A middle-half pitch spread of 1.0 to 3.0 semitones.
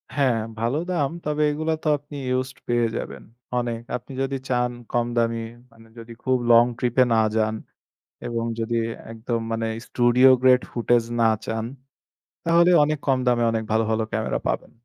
Yes: narrow, 2.4 semitones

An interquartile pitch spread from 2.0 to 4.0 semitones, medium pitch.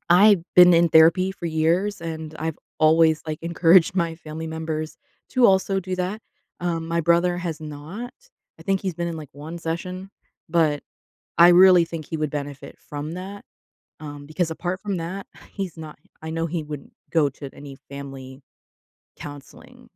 Yes: narrow, 2.6 semitones; medium, 165 Hz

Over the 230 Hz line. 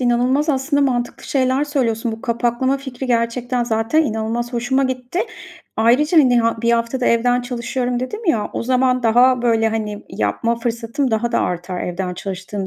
Yes: high, 240 Hz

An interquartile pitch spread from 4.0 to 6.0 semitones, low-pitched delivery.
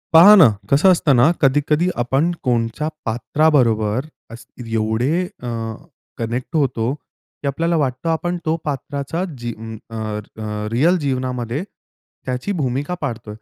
Yes: average, 4.6 semitones; low, 130 Hz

